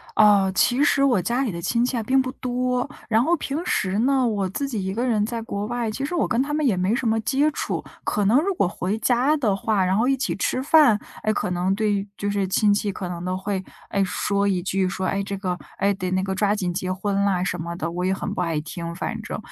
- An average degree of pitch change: Yes, average, 4.8 semitones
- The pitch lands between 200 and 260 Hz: Yes, high, 205 Hz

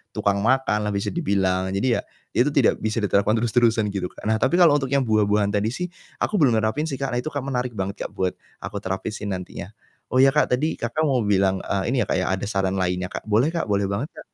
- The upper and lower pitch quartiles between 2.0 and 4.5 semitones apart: No, average, 5.0 semitones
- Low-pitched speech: Yes, low, 110 Hz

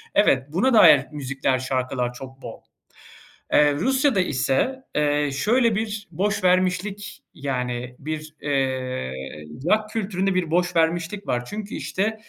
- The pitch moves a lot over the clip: Yes, wide, 7.5 semitones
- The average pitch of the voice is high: No, medium, 165 Hz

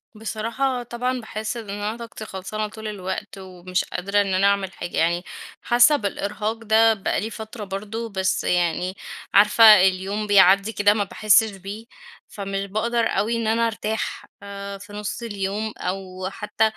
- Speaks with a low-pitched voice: No, high, 205 Hz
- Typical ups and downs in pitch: No, narrow, 2.3 semitones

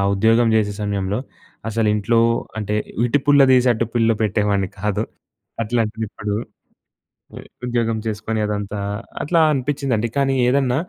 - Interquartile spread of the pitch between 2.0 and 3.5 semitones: Yes, average, 2.8 semitones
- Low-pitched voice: Yes, low, 110 Hz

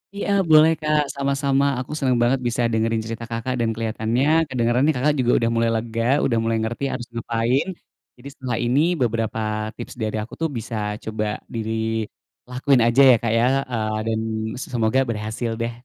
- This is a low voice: Yes, low, 120 Hz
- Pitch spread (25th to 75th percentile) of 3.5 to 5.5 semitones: No, narrow, 2.6 semitones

